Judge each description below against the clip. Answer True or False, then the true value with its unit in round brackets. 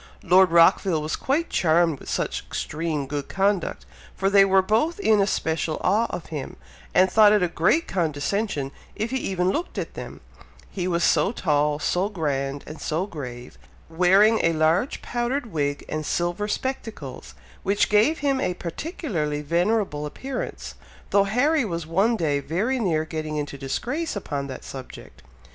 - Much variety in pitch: True (5.7 semitones)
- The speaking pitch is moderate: True (180 Hz)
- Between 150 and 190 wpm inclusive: True (160 wpm)